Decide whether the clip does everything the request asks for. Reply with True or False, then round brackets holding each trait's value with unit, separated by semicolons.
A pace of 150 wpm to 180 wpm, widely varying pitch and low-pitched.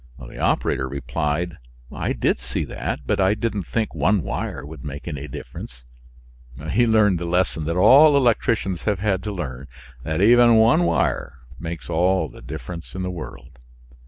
True (165 wpm; 6.2 semitones; 90 Hz)